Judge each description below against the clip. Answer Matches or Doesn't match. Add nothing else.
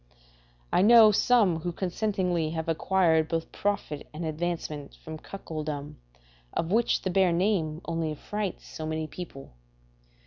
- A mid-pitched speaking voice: Matches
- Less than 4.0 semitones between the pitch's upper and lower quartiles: Matches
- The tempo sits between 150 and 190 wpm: Doesn't match